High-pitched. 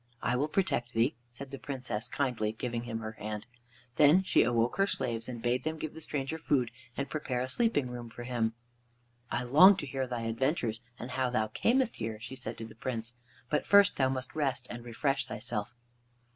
No: low, 125 Hz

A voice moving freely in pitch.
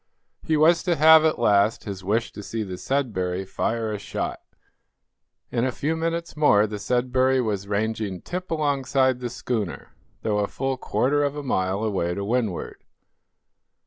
Yes: wide, 5.7 semitones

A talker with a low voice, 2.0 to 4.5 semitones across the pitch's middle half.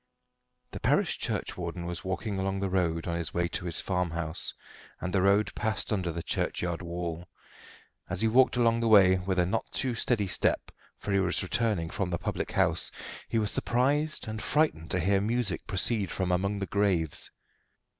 Yes: very low, 95 Hz; average, 3.6 semitones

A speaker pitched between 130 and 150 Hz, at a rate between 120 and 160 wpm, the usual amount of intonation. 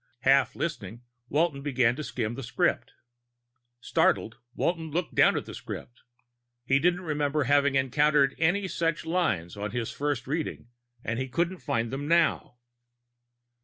Yes: medium, 140 Hz; average, 145 wpm; average, 4.7 semitones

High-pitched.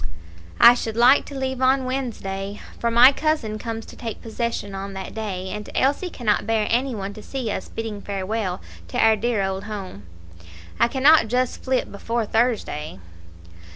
Yes: high, 225 Hz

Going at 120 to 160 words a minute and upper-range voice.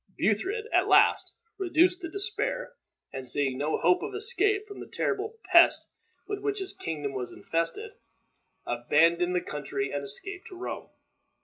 Yes: average, 150 wpm; very high, 335 Hz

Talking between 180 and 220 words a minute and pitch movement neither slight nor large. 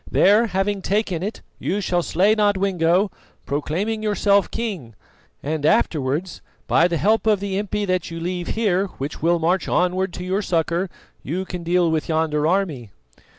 No: average, 160 wpm; average, 3.5 semitones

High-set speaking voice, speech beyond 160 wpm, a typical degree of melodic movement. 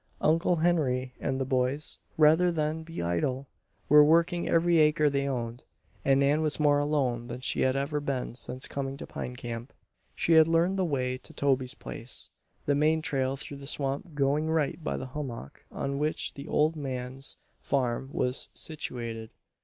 No: medium, 140 Hz; average, 175 wpm; average, 3.2 semitones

